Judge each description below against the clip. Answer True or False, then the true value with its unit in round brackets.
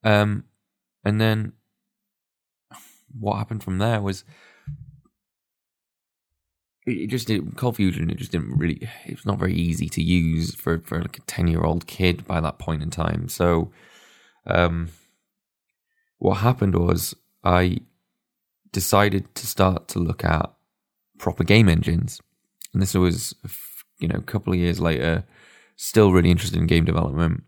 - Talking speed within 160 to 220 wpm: False (150 wpm)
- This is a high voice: False (95 Hz)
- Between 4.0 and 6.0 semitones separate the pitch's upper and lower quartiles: True (4.8 semitones)